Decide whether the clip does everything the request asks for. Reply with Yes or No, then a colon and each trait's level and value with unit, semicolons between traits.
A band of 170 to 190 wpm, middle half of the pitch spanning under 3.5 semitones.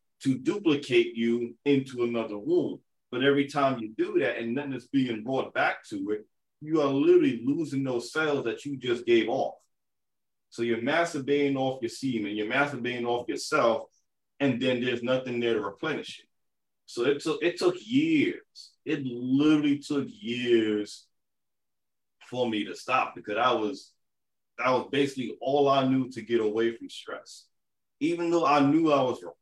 No: average, 175 wpm; average, 3.9 semitones